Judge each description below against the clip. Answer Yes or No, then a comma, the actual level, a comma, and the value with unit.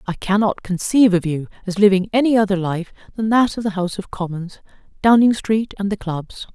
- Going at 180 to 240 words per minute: Yes, average, 200 wpm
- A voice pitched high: Yes, high, 200 Hz